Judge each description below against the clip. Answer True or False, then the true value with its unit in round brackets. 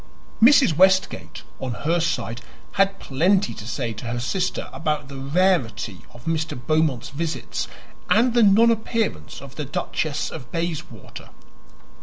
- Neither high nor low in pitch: True (155 Hz)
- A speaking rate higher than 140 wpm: False (135 wpm)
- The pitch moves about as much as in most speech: False (7.5 semitones)